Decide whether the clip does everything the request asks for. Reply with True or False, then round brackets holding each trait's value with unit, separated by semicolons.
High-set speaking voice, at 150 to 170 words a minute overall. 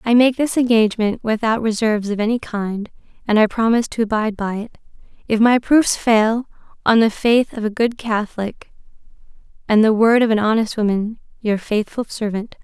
True (220 Hz; 165 wpm)